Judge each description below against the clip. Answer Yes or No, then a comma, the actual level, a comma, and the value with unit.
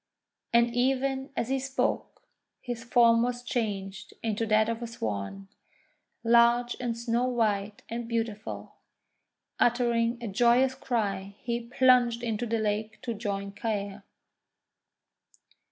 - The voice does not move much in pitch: Yes, narrow, 2.2 semitones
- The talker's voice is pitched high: Yes, high, 230 Hz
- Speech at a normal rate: No, slow, 120 wpm